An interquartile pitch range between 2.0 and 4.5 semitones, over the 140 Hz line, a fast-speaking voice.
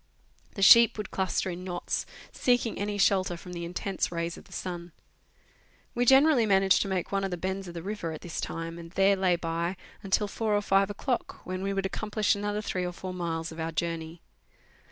Yes: average, 3.0 semitones; high, 190 Hz; fast, 215 wpm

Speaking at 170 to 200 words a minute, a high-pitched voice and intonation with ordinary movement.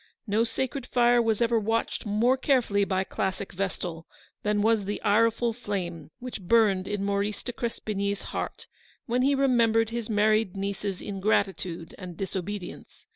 No: average, 145 wpm; high, 210 Hz; average, 3.0 semitones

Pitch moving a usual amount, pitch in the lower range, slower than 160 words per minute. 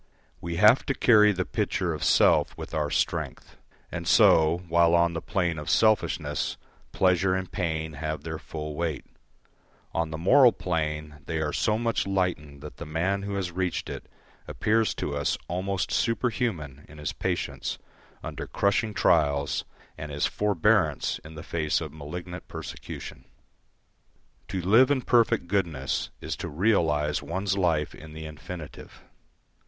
Yes: average, 4.1 semitones; very low, 85 Hz; average, 150 wpm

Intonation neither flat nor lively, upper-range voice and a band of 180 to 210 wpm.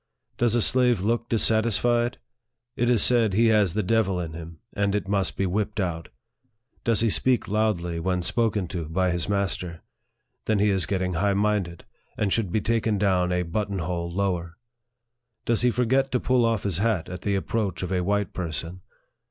No: average, 3.9 semitones; low, 100 Hz; average, 190 wpm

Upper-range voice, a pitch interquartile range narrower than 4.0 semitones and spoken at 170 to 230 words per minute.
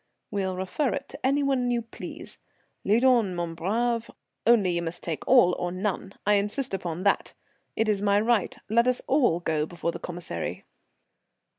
No: high, 205 Hz; average, 5.3 semitones; average, 175 wpm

